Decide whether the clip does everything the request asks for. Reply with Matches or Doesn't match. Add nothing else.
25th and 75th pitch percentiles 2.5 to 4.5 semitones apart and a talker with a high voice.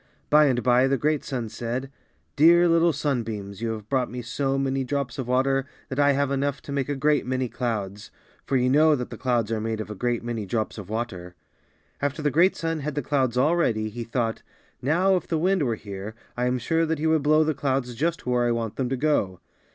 Doesn't match